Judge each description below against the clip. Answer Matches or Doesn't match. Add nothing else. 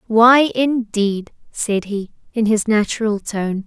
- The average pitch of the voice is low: Doesn't match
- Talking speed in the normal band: Doesn't match